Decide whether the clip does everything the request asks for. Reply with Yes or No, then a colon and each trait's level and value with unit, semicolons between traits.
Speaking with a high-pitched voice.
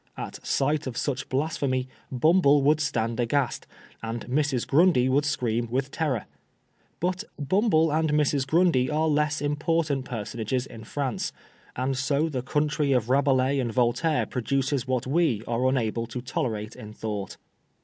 No: low, 135 Hz